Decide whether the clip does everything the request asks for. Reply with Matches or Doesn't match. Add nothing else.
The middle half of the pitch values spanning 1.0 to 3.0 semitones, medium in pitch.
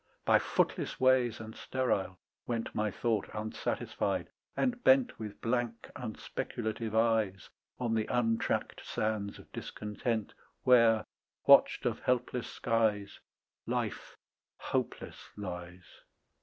Doesn't match